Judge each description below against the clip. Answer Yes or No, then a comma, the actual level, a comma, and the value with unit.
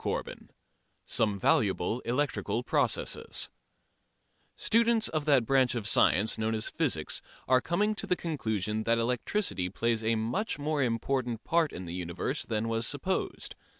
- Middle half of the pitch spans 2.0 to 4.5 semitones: No, average, 5.1 semitones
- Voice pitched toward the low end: Yes, low, 120 Hz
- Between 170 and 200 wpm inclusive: No, average, 150 wpm